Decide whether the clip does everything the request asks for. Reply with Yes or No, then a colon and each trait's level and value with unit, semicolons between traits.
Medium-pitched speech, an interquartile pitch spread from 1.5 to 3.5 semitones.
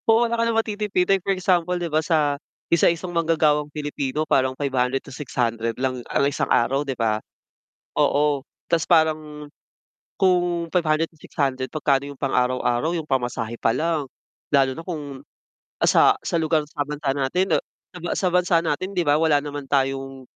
No: medium, 150 Hz; average, 3.9 semitones